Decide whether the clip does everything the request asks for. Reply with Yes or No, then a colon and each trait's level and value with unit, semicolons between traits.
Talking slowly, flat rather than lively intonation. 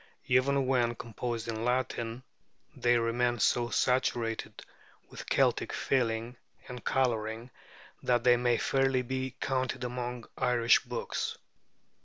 Yes: slow, 115 wpm; narrow, 1.5 semitones